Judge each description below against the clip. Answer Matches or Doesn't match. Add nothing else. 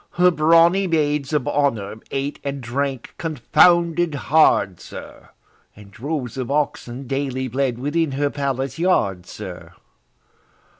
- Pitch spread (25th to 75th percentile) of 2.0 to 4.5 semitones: Matches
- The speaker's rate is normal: Doesn't match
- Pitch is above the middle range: Doesn't match